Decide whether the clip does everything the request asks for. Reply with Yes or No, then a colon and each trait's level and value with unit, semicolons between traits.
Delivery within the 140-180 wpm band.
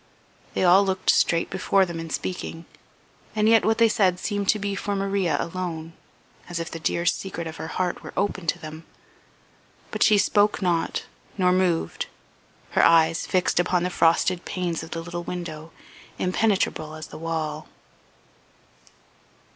Yes: average, 160 wpm